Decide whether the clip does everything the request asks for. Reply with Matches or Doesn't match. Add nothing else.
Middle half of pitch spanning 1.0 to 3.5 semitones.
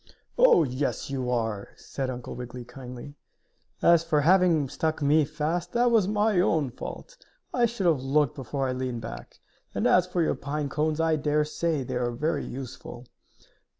Doesn't match